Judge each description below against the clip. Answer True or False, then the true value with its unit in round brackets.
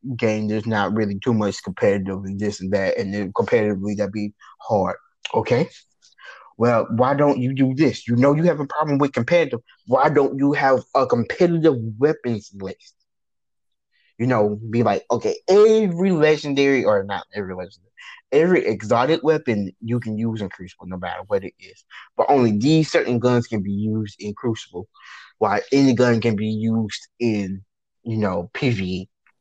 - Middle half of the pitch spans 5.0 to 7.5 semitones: True (5.3 semitones)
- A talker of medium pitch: False (115 Hz)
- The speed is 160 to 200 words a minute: True (170 wpm)